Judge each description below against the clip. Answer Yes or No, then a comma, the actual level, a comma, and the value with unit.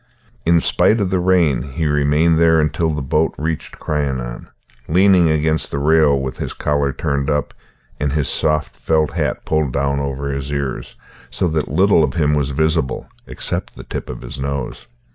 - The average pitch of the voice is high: No, very low, 75 Hz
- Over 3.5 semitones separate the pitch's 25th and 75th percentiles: No, narrow, 2.5 semitones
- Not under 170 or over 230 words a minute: Yes, average, 180 wpm